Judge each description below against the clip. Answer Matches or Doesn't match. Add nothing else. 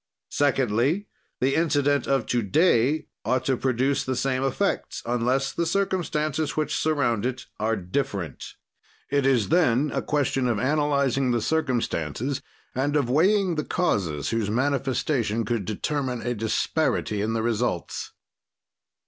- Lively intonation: Doesn't match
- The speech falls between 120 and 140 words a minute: Matches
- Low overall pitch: Matches